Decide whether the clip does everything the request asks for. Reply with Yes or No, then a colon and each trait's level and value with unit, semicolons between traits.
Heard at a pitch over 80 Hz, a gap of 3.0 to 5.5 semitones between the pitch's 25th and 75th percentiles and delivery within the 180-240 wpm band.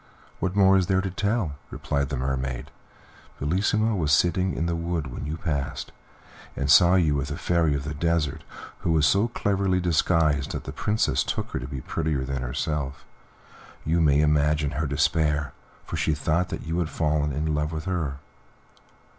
No: very low, 75 Hz; average, 3.4 semitones; average, 185 wpm